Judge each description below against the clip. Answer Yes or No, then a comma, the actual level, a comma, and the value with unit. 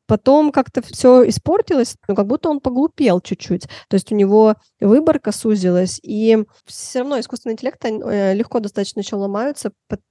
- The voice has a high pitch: Yes, high, 225 Hz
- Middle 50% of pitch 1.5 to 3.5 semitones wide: No, average, 4.2 semitones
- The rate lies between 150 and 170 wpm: Yes, average, 155 wpm